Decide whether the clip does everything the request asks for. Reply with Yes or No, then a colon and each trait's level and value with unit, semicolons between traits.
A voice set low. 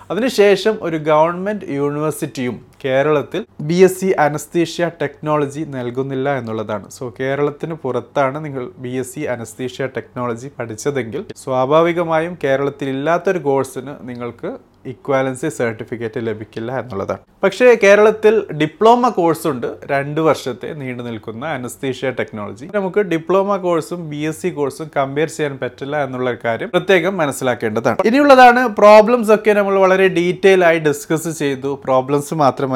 No: medium, 145 Hz